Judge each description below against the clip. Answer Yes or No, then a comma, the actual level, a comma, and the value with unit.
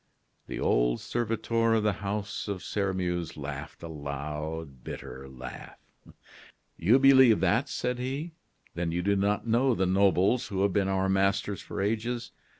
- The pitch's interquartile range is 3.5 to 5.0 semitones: No, wide, 5.5 semitones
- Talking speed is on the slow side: No, average, 150 wpm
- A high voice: No, low, 100 Hz